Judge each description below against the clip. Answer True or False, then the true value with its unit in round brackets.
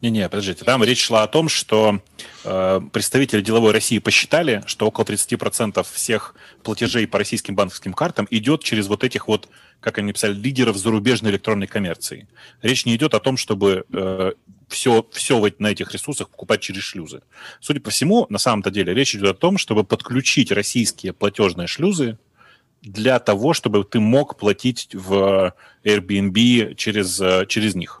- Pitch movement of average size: True (3.1 semitones)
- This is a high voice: False (110 Hz)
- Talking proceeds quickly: True (165 wpm)